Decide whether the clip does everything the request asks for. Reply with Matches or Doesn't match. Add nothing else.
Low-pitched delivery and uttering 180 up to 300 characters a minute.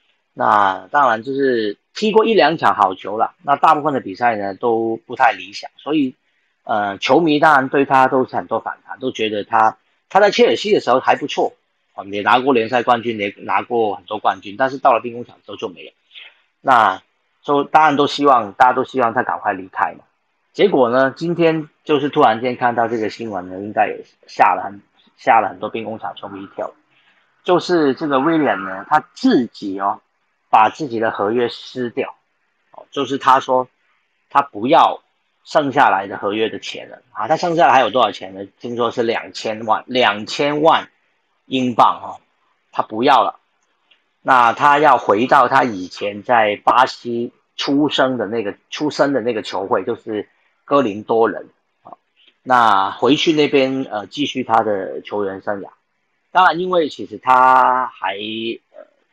Matches